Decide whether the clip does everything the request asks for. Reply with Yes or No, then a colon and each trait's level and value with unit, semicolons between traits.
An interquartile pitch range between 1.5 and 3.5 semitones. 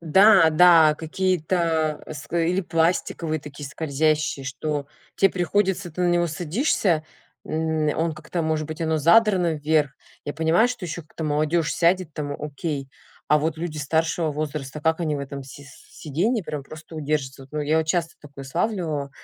Yes: narrow, 2.4 semitones